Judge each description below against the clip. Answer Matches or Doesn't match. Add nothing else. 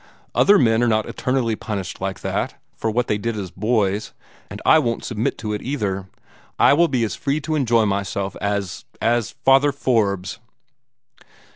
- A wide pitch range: Doesn't match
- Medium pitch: Doesn't match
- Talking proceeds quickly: Doesn't match